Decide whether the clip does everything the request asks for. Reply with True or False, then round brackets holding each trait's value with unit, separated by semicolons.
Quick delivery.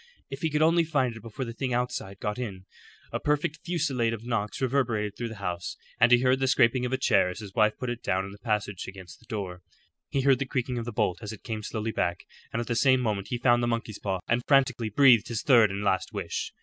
True (255 wpm)